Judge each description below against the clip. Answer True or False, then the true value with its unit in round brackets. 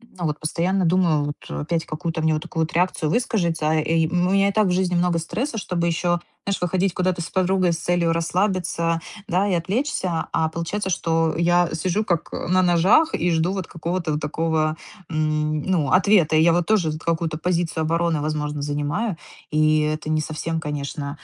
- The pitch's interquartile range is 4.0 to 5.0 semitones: False (2.6 semitones)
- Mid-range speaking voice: True (170 Hz)